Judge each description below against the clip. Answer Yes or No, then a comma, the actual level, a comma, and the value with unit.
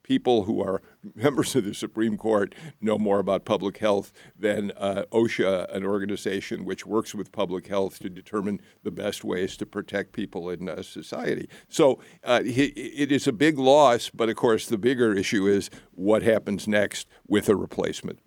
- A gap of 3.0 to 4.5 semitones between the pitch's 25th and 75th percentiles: No, narrow, 2.6 semitones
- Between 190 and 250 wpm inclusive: No, average, 180 wpm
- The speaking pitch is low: Yes, low, 105 Hz